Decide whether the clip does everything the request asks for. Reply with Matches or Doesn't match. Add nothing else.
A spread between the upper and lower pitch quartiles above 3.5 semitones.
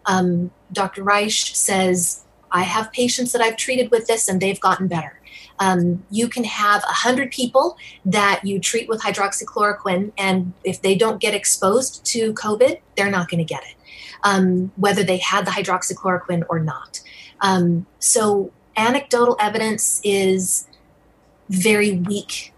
Doesn't match